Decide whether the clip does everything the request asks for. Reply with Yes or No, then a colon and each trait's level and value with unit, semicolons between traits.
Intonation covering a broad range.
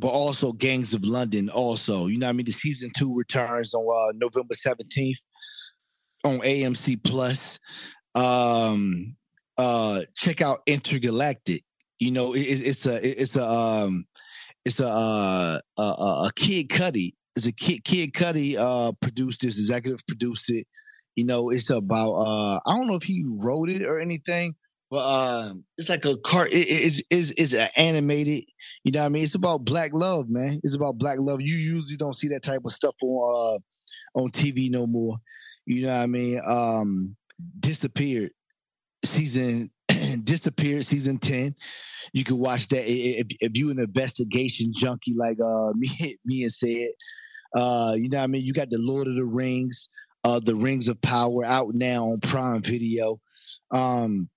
No: average, 3.5 semitones